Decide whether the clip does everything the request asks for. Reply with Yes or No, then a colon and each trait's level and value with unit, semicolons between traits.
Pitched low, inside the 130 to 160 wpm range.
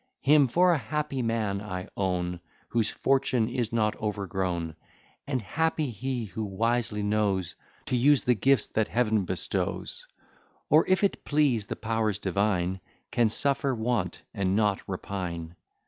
Yes: low, 110 Hz; average, 145 wpm